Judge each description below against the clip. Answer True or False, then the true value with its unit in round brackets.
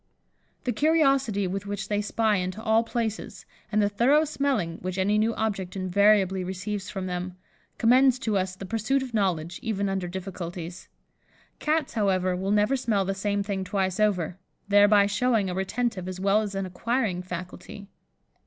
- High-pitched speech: True (200 Hz)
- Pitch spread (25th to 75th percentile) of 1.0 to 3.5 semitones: True (3.0 semitones)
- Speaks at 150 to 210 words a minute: True (165 wpm)